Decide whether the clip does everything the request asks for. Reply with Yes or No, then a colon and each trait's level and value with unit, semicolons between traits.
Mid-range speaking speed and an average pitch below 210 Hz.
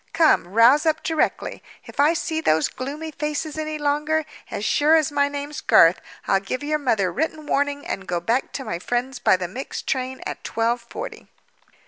No: average, 185 wpm; very high, 285 Hz